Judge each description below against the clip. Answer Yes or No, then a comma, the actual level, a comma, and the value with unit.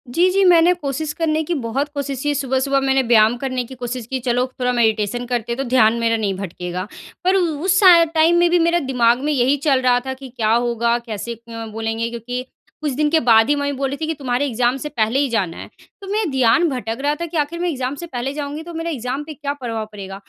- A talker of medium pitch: No, very high, 260 Hz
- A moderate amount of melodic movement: Yes, average, 4.2 semitones